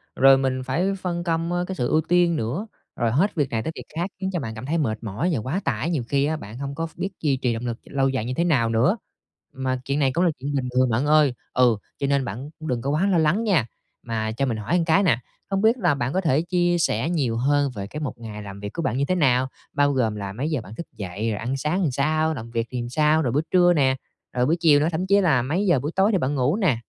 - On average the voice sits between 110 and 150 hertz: Yes, medium, 140 Hz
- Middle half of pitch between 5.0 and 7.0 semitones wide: Yes, wide, 5.4 semitones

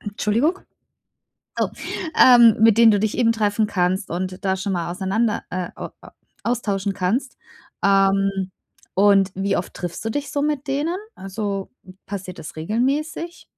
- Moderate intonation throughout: Yes, average, 3.6 semitones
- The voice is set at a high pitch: Yes, high, 205 Hz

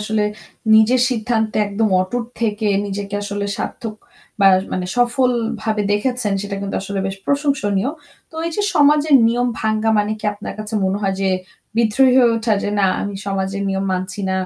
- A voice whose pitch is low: No, high, 215 Hz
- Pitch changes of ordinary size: Yes, average, 3.2 semitones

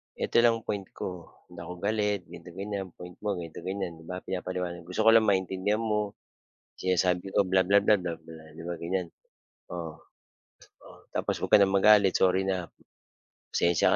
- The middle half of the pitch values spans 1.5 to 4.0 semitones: Yes, narrow, 2.4 semitones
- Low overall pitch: Yes, very low, 95 Hz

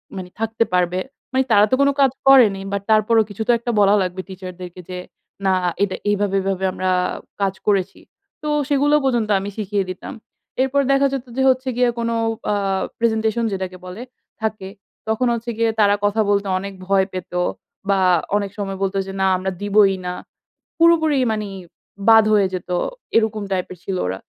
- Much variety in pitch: No, average, 3.3 semitones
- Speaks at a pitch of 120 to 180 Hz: No, high, 205 Hz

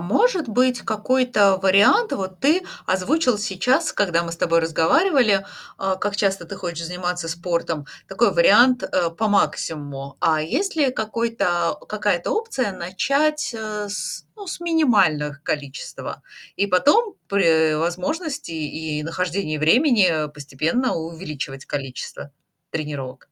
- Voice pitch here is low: No, high, 190 Hz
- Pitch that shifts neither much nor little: No, wide, 7.5 semitones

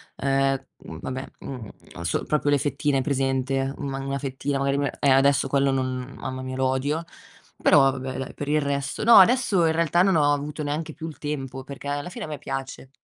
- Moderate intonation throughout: No, narrow, 1.8 semitones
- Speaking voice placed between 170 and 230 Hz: No, medium, 140 Hz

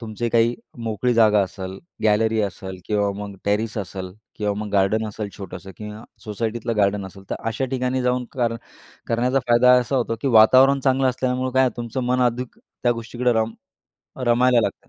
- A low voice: Yes, low, 115 Hz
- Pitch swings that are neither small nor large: Yes, average, 3.1 semitones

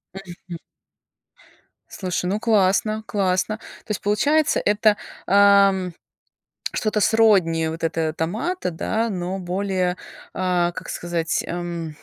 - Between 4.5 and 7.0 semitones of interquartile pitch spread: No, average, 3.3 semitones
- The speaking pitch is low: No, medium, 185 Hz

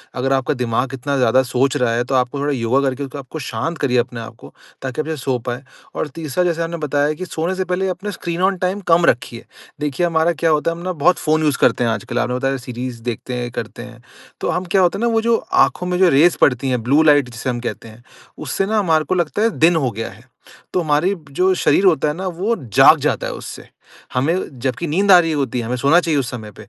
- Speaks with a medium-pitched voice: Yes, medium, 145 Hz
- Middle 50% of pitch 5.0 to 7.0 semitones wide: Yes, wide, 5.6 semitones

